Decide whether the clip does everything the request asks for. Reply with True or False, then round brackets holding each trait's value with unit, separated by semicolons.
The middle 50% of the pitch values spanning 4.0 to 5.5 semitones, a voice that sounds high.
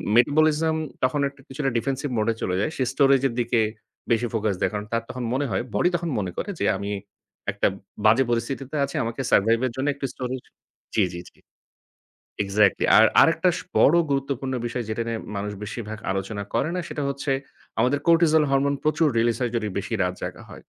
False (4.4 semitones; 125 Hz)